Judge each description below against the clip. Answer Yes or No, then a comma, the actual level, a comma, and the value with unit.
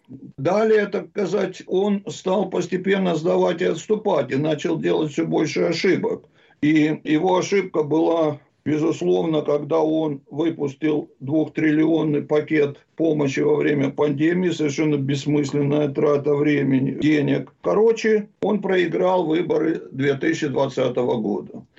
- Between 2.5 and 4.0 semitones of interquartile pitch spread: Yes, average, 3.6 semitones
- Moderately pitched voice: Yes, medium, 155 Hz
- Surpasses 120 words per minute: No, slow, 110 wpm